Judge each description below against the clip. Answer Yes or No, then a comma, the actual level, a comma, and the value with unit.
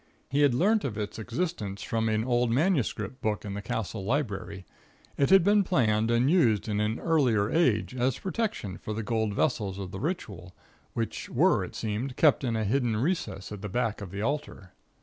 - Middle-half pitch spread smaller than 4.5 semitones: No, average, 5.2 semitones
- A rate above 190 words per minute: Yes, average, 200 wpm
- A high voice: No, low, 115 Hz